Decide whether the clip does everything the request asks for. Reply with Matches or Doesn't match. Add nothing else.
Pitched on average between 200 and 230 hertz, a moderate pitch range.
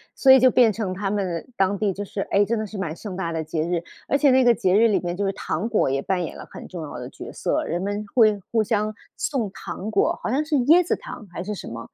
Matches